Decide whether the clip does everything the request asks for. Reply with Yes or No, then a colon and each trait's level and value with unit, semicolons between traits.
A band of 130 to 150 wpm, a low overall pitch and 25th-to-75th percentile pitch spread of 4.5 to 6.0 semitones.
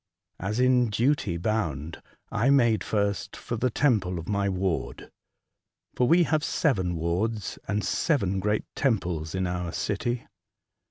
Yes: average, 140 wpm; low, 105 Hz; average, 5.1 semitones